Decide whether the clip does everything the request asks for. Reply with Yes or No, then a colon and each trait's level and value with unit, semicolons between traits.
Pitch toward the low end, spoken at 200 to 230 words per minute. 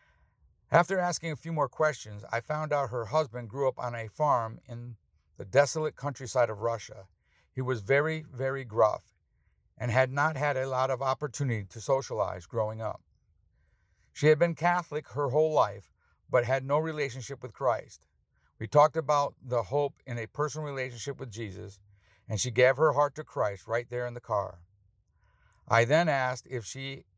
No: low, 130 Hz; average, 175 wpm